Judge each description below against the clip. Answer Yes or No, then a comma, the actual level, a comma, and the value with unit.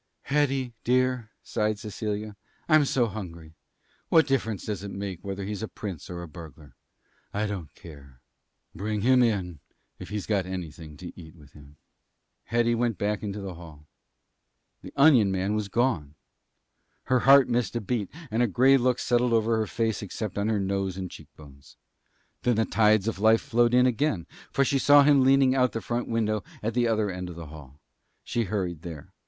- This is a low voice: Yes, low, 105 Hz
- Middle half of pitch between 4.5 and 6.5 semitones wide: Yes, average, 4.9 semitones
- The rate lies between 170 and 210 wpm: Yes, average, 190 wpm